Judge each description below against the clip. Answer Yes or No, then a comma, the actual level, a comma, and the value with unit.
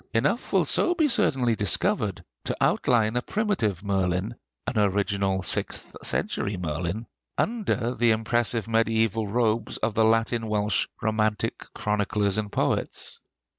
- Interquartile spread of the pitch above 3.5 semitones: No, narrow, 2.5 semitones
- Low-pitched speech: Yes, low, 110 Hz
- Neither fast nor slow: No, slow, 130 wpm